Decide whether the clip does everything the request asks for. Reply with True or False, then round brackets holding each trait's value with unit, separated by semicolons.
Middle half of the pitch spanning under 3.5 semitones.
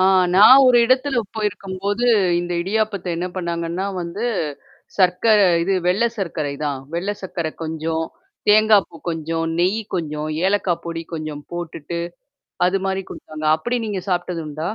False (3.8 semitones)